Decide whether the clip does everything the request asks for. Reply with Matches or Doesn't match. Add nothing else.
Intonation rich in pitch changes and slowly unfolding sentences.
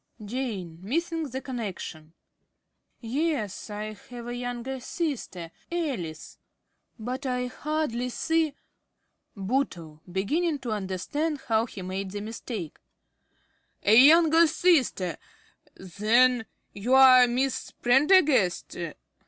Matches